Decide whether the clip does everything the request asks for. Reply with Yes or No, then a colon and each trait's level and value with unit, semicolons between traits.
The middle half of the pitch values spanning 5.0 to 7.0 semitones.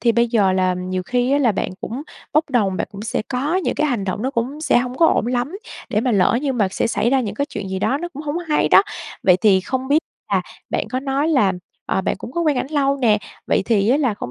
Yes: wide, 5.4 semitones